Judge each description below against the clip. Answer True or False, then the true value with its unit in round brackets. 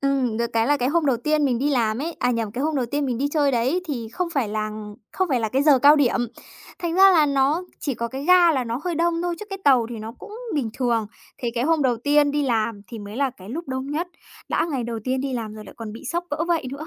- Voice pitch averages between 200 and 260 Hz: False (270 Hz)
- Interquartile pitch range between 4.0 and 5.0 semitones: True (4.5 semitones)